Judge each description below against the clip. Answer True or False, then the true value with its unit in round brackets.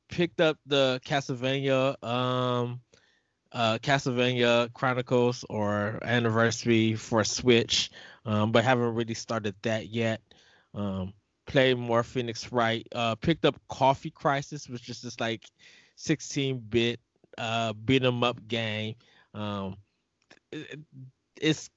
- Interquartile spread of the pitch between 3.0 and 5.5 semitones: False (2.6 semitones)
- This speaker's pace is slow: True (115 wpm)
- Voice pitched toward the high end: False (120 Hz)